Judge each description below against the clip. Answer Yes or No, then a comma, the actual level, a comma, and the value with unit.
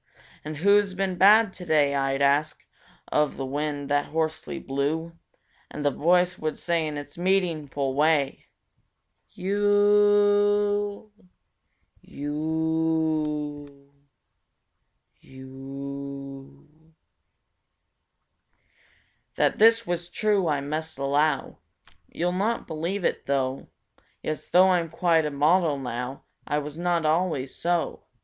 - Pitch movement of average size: Yes, average, 4.2 semitones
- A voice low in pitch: No, medium, 155 Hz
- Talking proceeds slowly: Yes, slow, 105 wpm